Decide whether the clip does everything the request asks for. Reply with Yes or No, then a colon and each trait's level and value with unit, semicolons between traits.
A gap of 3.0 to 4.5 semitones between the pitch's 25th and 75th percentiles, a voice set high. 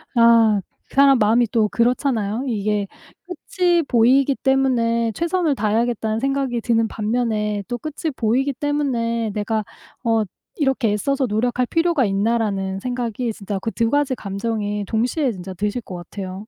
Yes: average, 4.0 semitones; high, 230 Hz